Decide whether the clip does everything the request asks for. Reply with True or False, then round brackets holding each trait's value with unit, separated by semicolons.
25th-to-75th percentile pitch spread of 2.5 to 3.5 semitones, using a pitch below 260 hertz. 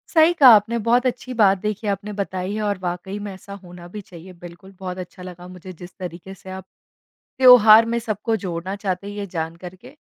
True (2.9 semitones; 190 Hz)